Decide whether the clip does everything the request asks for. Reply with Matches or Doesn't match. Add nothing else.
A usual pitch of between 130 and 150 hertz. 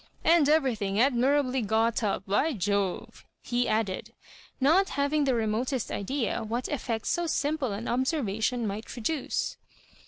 Doesn't match